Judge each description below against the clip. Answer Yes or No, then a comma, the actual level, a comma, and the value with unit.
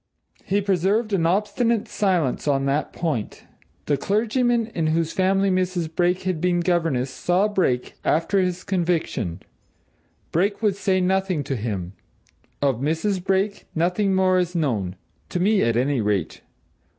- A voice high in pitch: No, medium, 180 Hz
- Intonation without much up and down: No, average, 4.8 semitones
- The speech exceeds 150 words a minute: No, average, 145 wpm